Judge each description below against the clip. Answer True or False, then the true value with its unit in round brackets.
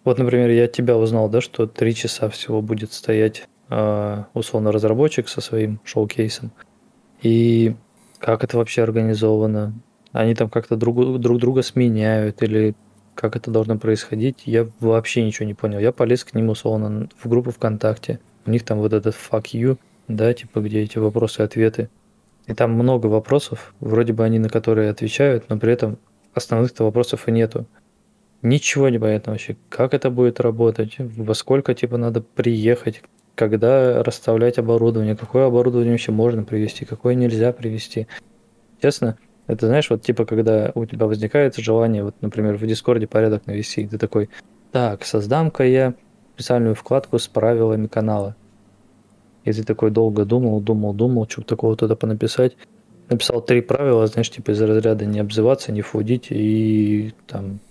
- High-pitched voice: False (115 Hz)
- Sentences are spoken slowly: False (160 wpm)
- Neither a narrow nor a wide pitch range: False (1.8 semitones)